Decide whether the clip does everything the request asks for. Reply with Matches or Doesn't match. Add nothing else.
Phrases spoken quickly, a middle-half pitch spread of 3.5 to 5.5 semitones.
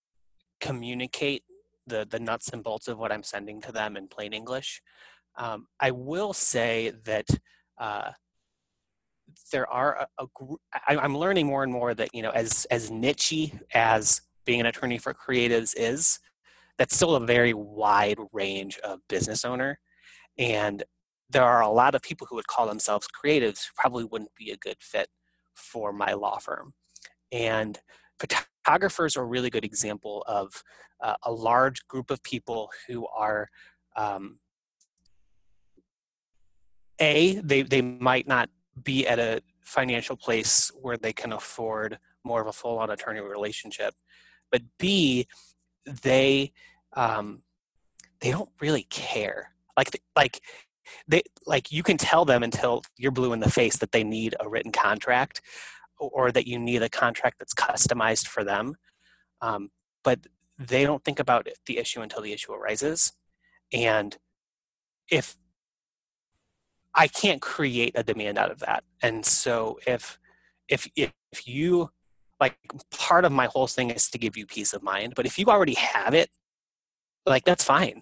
Doesn't match